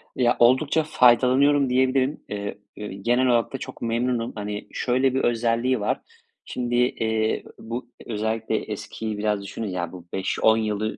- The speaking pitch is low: Yes, low, 115 Hz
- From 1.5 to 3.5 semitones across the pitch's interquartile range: Yes, average, 2.8 semitones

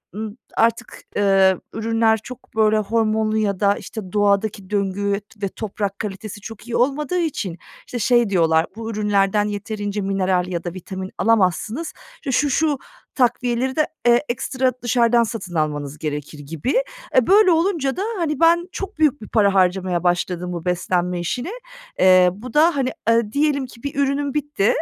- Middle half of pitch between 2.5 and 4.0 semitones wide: No, average, 5.1 semitones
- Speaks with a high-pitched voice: Yes, high, 215 Hz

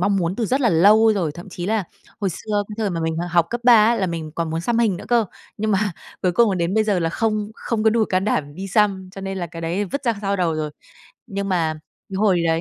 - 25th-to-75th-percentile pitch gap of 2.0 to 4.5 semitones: Yes, average, 3.9 semitones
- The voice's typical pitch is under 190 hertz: No, high, 195 Hz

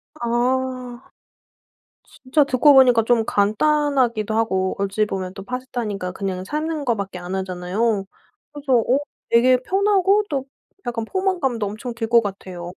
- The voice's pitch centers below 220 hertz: No, high, 235 Hz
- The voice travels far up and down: No, average, 4.8 semitones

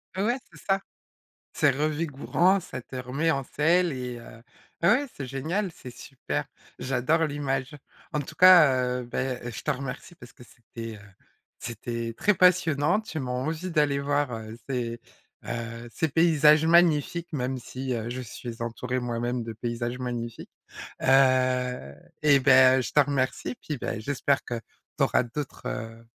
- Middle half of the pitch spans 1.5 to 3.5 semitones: No, average, 3.9 semitones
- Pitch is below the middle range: Yes, low, 130 Hz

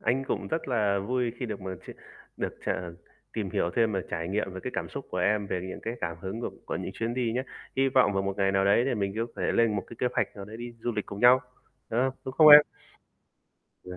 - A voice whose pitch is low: Yes, low, 110 Hz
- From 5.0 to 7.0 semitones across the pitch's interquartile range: No, average, 3.9 semitones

